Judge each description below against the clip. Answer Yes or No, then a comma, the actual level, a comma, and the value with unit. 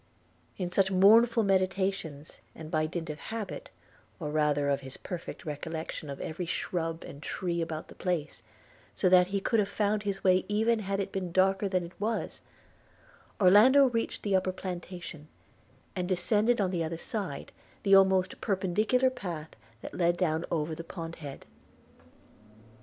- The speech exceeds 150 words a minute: Yes, average, 160 wpm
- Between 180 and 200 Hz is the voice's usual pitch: Yes, medium, 185 Hz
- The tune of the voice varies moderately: Yes, average, 3.3 semitones